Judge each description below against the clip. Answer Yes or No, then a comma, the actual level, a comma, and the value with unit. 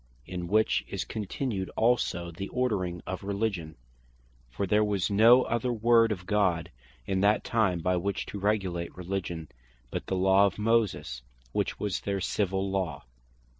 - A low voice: Yes, low, 100 Hz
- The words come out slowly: No, average, 155 wpm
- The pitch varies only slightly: No, average, 3.1 semitones